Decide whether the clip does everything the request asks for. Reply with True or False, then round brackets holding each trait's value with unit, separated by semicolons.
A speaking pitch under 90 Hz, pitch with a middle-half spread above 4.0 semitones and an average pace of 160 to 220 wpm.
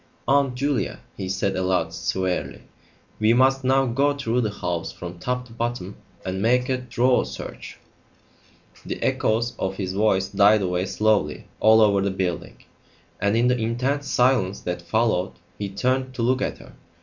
False (110 Hz; 4.9 semitones; 165 wpm)